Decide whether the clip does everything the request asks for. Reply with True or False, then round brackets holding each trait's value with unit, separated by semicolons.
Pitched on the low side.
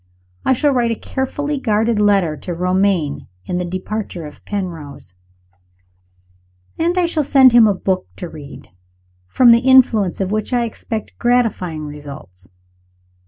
False (205 Hz)